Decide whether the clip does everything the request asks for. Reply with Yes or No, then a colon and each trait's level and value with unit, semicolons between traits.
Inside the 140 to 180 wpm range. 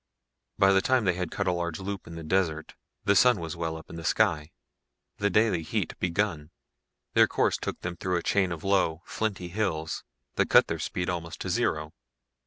No: average, 200 wpm